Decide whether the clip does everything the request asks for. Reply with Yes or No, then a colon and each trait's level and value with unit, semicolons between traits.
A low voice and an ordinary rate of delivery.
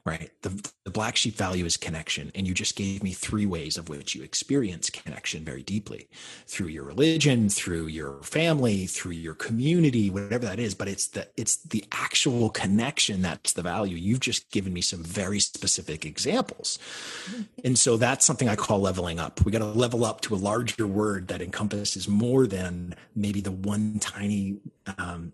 Yes: low, 100 Hz; average, 185 wpm